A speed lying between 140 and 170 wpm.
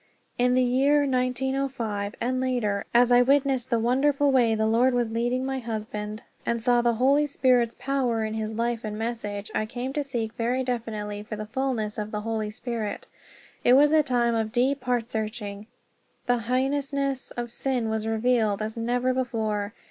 No: average, 180 wpm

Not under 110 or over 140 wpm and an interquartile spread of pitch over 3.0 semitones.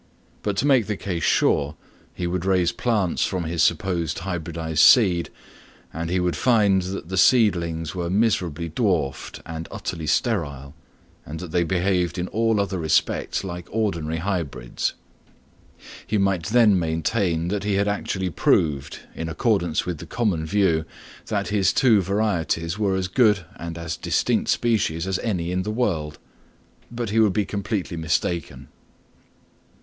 No: average, 155 wpm; average, 3.7 semitones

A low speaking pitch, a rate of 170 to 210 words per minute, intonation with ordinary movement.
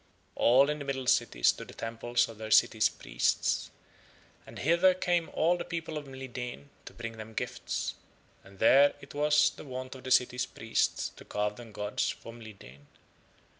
Yes: low, 125 Hz; average, 175 wpm; average, 4.4 semitones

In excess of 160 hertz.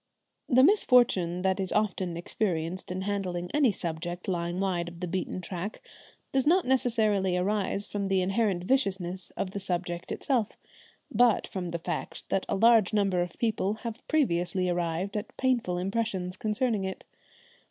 Yes: high, 190 Hz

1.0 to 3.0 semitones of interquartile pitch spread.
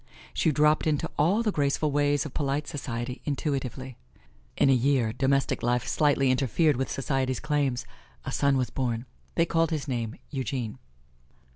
Yes: narrow, 2.6 semitones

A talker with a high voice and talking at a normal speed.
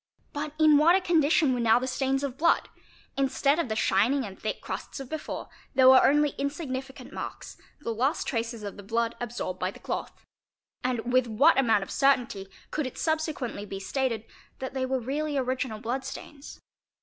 Yes: very high, 260 Hz; average, 185 wpm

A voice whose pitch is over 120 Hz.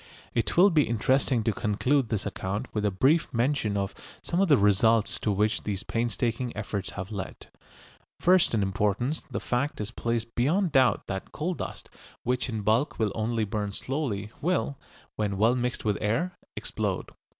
No: low, 115 Hz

